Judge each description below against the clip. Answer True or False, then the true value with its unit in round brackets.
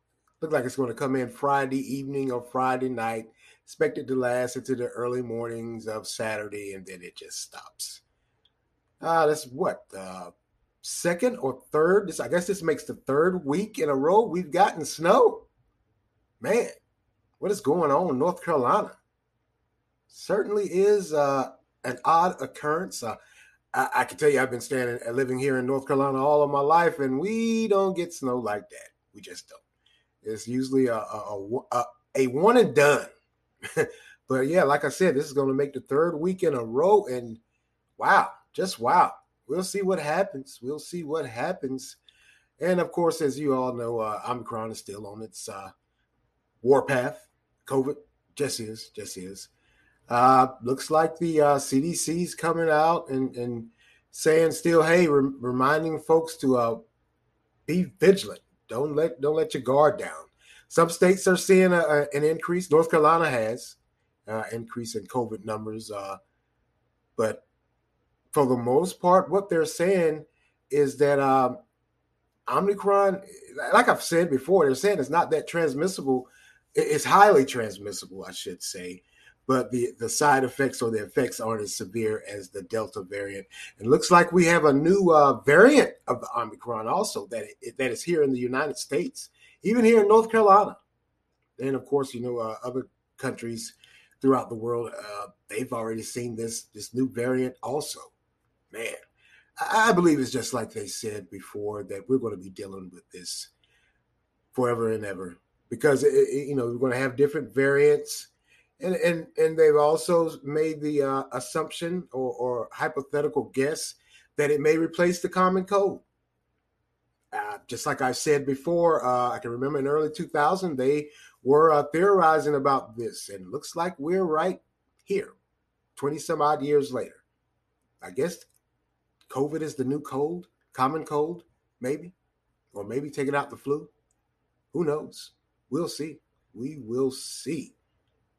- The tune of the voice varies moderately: False (5.8 semitones)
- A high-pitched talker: False (140 Hz)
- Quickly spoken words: False (170 wpm)